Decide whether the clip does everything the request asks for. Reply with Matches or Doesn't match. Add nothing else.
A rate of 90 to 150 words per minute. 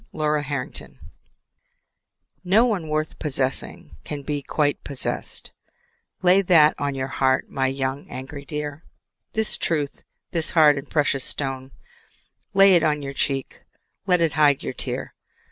Matches